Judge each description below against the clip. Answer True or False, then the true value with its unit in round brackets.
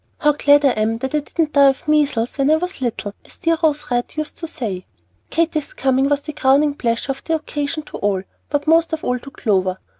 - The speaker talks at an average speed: False (230 wpm)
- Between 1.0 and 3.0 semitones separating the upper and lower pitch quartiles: False (3.8 semitones)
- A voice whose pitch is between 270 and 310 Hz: True (285 Hz)